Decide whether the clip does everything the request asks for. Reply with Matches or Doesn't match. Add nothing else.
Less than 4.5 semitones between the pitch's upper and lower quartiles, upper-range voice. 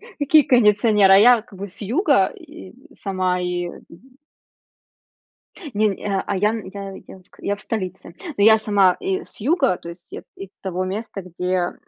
Matches